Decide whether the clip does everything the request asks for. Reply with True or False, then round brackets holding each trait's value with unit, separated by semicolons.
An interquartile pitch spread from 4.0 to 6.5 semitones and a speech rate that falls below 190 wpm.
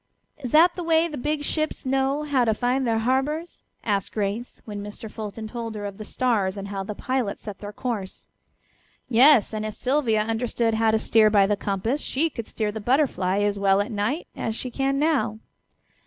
False (4.5 semitones; 200 wpm)